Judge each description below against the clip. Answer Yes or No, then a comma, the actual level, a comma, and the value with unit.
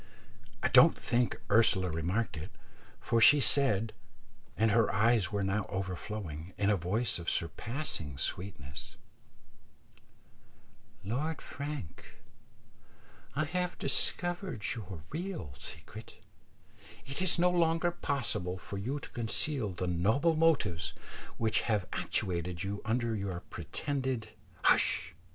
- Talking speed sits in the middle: No, slow, 120 wpm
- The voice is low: Yes, low, 110 Hz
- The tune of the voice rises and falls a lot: Yes, wide, 7.2 semitones